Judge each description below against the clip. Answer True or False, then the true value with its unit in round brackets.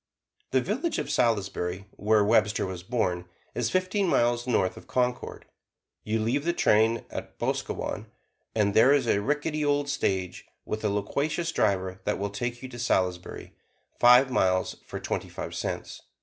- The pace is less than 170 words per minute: True (160 wpm)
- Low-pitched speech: True (115 Hz)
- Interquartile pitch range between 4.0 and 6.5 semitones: True (5.1 semitones)